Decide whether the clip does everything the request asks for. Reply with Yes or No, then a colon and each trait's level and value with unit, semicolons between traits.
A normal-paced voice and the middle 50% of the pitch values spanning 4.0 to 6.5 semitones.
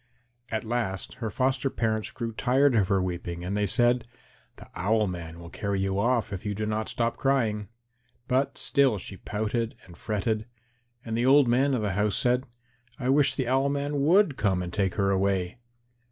Yes: average, 190 wpm; average, 4.6 semitones